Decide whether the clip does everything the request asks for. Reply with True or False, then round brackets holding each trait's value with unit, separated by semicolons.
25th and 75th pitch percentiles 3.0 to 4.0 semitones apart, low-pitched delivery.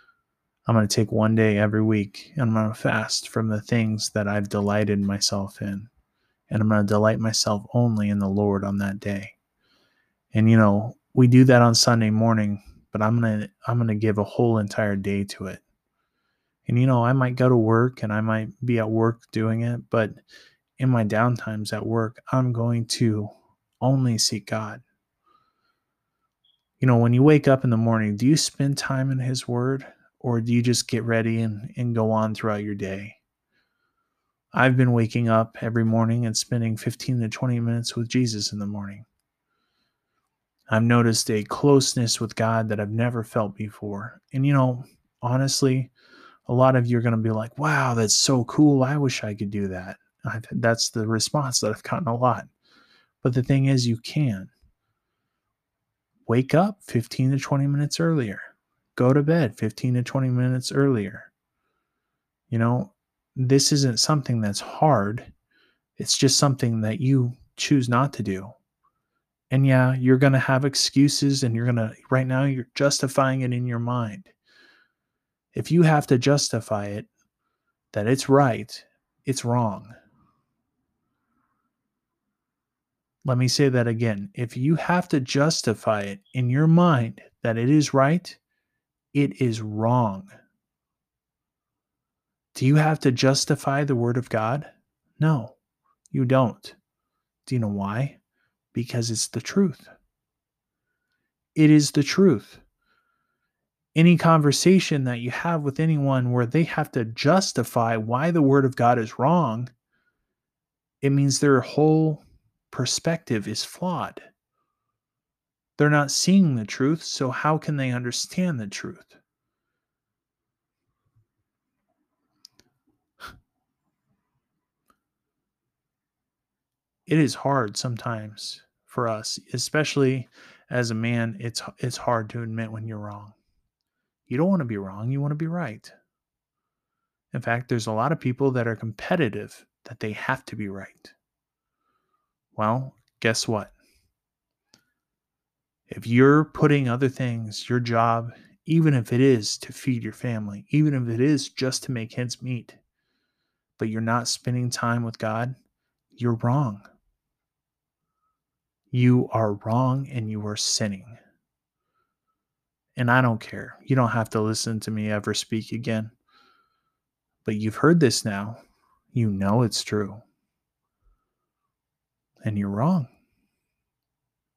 True (3.7 semitones; 120 Hz)